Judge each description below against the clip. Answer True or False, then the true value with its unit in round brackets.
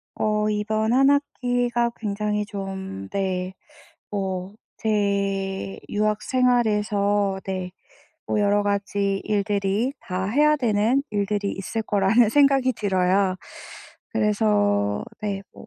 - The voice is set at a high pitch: True (205 Hz)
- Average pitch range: False (2.1 semitones)